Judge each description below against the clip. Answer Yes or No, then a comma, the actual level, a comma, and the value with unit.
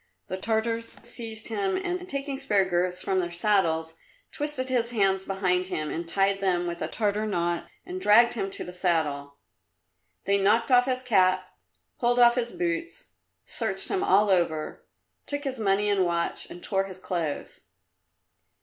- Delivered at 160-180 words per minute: Yes, average, 165 wpm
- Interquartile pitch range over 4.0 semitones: Yes, average, 4.9 semitones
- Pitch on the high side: Yes, high, 200 Hz